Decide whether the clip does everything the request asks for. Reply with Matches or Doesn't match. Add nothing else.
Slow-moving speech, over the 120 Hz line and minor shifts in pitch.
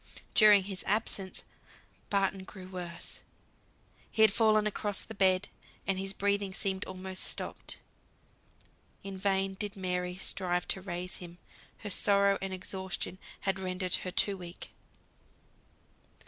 Matches